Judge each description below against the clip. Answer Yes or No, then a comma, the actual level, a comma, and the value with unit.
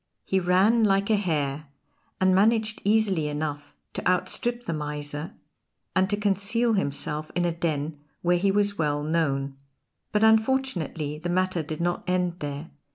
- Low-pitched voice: No, medium, 175 Hz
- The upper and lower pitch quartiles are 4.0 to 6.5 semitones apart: Yes, average, 5.2 semitones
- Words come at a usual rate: Yes, average, 155 wpm